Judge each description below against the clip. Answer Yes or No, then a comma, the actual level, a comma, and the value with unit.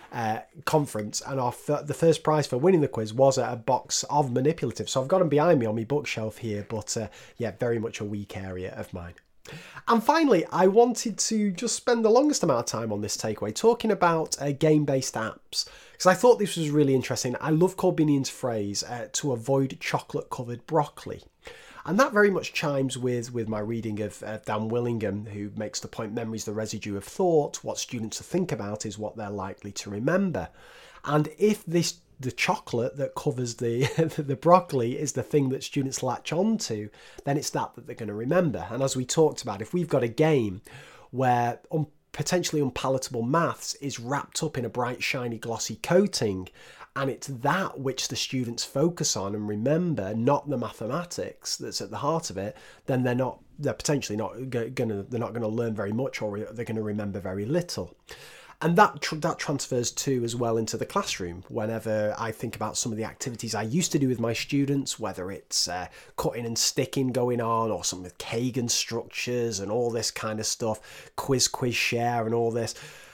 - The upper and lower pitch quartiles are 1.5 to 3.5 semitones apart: No, average, 5.2 semitones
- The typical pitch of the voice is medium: No, low, 125 Hz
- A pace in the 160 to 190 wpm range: No, fast, 205 wpm